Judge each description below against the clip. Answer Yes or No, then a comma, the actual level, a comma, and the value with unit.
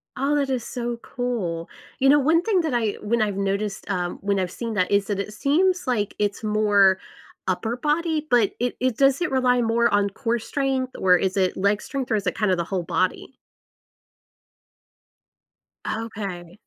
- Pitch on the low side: No, high, 225 Hz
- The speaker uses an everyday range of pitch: Yes, average, 4.7 semitones